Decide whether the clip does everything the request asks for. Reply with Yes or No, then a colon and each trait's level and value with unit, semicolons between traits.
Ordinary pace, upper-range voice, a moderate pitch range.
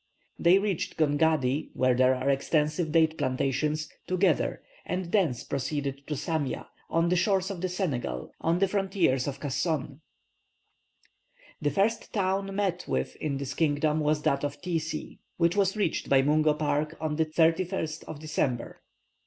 No: average, 155 wpm; medium, 155 Hz; average, 4.1 semitones